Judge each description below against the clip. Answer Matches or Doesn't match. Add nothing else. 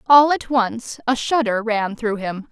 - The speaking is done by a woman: Matches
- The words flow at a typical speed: Matches